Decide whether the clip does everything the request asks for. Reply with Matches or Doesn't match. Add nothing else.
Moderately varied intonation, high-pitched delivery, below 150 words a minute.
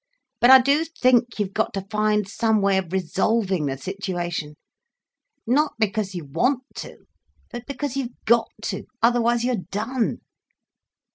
Matches